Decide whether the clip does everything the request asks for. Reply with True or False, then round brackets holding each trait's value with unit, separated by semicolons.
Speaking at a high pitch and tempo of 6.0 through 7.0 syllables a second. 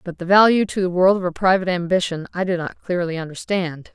False (180 Hz; 6.1 syllables/s)